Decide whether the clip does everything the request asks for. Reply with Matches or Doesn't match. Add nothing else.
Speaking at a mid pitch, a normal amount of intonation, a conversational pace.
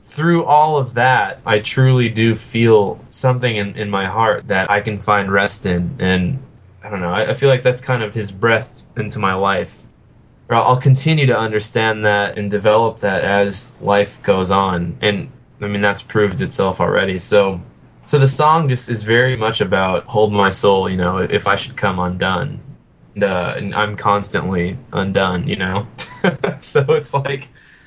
Doesn't match